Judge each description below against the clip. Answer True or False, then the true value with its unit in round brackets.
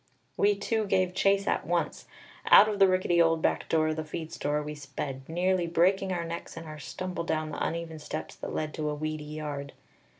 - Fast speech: True (210 wpm)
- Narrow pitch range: False (3.2 semitones)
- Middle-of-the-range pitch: True (165 Hz)